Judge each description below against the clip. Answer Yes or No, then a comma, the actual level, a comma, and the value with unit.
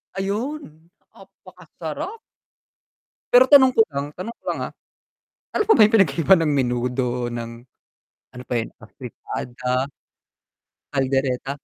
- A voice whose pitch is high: No, medium, 155 Hz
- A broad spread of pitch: Yes, wide, 9.0 semitones